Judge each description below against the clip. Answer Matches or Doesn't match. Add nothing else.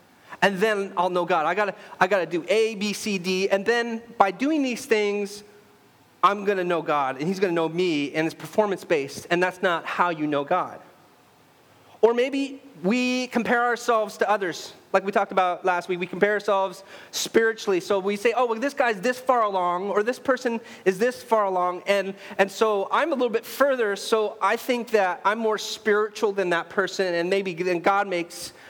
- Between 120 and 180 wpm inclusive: Doesn't match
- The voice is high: Matches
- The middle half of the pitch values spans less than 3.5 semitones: Doesn't match